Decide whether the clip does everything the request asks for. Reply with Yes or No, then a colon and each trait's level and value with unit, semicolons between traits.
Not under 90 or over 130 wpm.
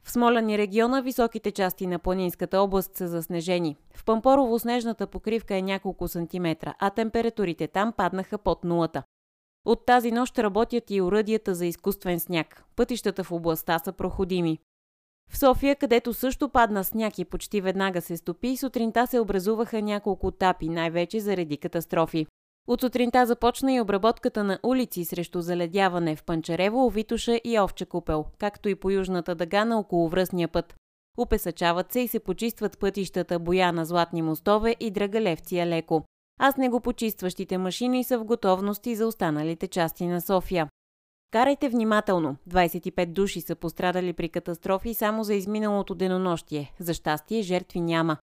No: average, 150 wpm